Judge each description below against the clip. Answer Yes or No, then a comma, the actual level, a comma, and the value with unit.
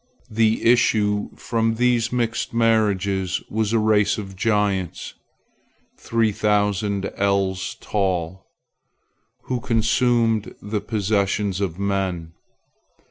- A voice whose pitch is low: Yes, low, 105 Hz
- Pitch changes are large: No, narrow, 2.6 semitones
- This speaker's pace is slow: Yes, slow, 95 wpm